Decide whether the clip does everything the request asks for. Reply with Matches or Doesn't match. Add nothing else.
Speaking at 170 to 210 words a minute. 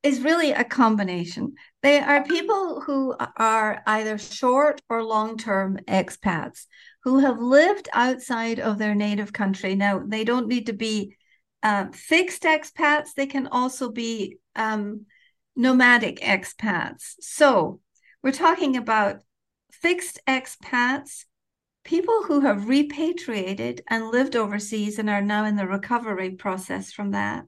Doesn't match